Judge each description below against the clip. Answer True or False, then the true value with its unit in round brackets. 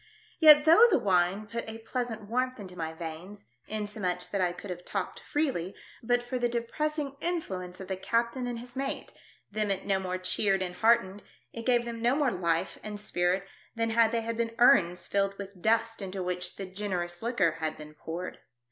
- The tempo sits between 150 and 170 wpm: False (195 wpm)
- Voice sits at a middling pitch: False (210 Hz)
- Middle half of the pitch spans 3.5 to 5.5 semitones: True (4.5 semitones)